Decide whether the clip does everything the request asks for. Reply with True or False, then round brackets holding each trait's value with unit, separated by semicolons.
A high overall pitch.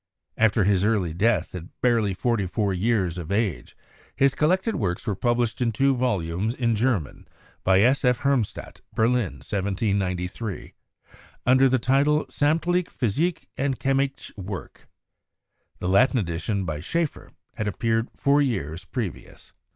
False (110 Hz)